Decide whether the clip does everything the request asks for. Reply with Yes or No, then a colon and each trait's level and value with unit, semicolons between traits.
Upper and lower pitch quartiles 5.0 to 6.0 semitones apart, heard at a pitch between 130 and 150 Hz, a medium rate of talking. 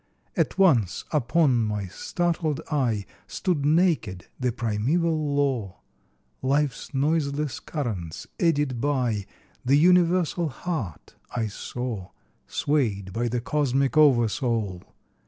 No: average, 5.3 semitones; low, 135 Hz; slow, 100 wpm